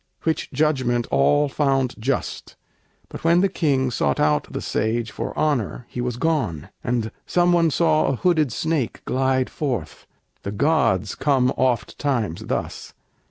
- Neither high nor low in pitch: No, low, 130 Hz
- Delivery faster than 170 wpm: No, average, 150 wpm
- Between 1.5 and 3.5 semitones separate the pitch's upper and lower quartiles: No, average, 4.7 semitones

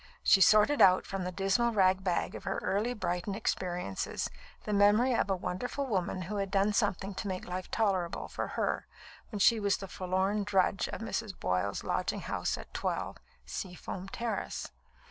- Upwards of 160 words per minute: Yes, average, 175 wpm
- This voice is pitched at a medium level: No, high, 195 Hz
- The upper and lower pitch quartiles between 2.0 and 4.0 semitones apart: Yes, narrow, 2.4 semitones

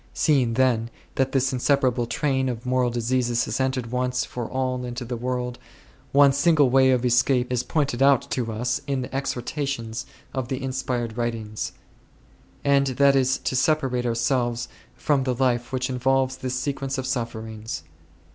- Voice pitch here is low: Yes, low, 125 Hz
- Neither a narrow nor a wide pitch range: No, narrow, 1.8 semitones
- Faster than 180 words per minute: No, average, 160 wpm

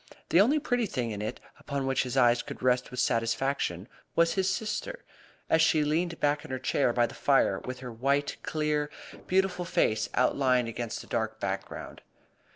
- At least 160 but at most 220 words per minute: Yes, average, 180 wpm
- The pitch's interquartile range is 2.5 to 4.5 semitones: No, average, 5.2 semitones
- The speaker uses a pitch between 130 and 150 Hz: Yes, low, 135 Hz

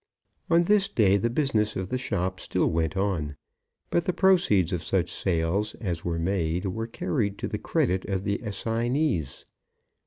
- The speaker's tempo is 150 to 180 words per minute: Yes, average, 165 wpm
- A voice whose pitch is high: No, low, 100 Hz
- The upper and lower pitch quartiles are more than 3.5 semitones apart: Yes, average, 4.8 semitones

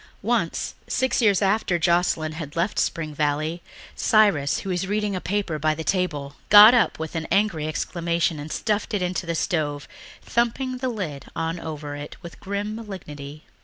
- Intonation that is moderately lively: Yes, average, 4.9 semitones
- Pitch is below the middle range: No, medium, 170 Hz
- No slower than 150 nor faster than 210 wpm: Yes, average, 170 wpm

